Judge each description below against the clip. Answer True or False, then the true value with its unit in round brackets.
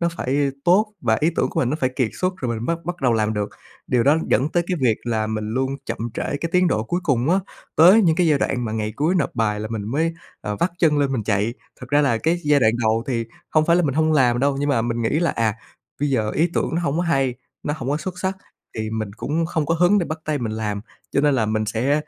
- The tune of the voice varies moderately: False (6.4 semitones)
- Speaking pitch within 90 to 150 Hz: True (140 Hz)